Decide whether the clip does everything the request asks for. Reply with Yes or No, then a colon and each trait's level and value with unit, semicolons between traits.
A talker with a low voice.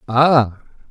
Yes: low, 130 Hz